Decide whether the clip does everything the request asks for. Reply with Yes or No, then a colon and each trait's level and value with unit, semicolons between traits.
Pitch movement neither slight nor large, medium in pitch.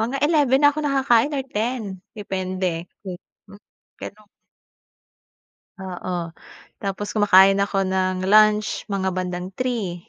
No: average, 3.7 semitones; high, 195 Hz